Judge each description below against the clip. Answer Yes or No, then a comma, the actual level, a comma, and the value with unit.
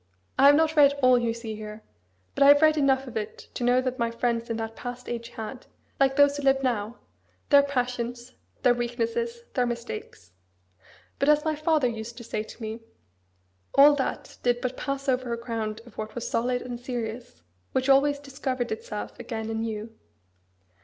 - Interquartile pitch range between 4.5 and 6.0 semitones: No, average, 3.1 semitones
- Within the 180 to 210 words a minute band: Yes, average, 185 wpm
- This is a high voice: Yes, high, 245 Hz